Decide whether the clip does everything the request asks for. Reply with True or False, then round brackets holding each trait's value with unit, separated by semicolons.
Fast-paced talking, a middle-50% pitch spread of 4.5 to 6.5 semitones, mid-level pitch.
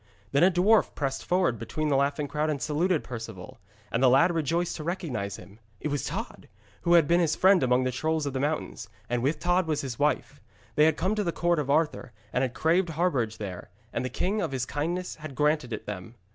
True (230 wpm; 5.0 semitones; 150 Hz)